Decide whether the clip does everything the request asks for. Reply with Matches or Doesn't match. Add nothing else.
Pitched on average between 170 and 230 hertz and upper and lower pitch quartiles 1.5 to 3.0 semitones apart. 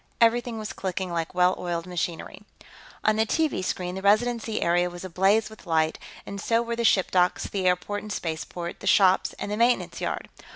Doesn't match